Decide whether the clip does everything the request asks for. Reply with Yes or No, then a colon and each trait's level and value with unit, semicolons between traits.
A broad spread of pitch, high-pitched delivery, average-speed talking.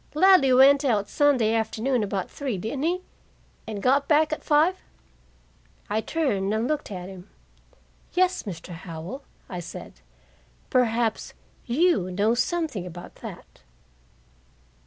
No: wide, 6.7 semitones; high, 240 Hz; slow, 125 wpm